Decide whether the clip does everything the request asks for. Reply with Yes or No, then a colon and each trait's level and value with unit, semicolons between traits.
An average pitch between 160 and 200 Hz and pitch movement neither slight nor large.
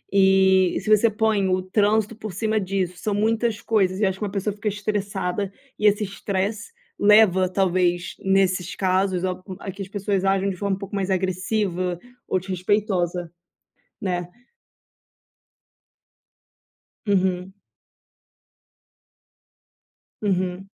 No: high, 195 Hz; narrow, 1.8 semitones